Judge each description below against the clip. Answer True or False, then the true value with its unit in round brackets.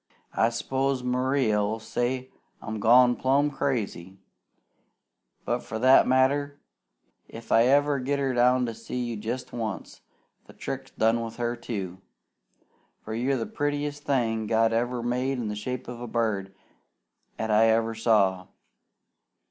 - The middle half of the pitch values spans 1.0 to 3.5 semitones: True (2.7 semitones)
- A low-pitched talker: True (120 Hz)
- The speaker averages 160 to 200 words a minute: False (150 wpm)